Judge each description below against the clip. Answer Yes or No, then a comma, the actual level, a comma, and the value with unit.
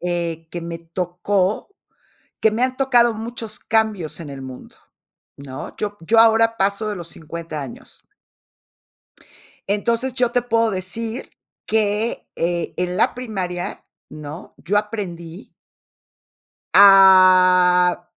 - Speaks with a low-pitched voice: No, high, 190 Hz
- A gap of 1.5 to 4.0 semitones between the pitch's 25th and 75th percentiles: No, average, 4.5 semitones